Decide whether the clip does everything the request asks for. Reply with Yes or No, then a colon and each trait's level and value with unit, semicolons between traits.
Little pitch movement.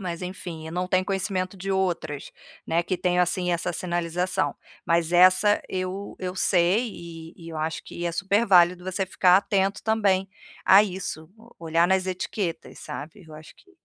Yes: narrow, 2.0 semitones